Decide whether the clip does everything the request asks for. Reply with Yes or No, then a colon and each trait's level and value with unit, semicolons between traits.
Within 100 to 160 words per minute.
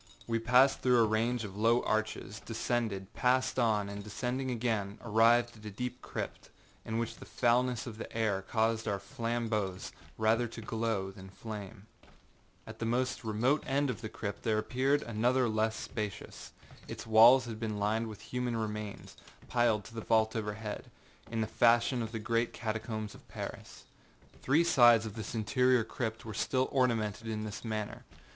No: average, 170 wpm